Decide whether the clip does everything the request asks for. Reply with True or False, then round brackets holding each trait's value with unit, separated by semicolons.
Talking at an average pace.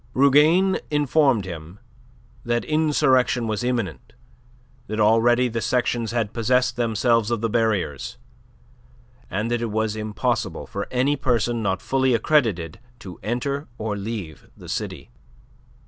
False (130 wpm)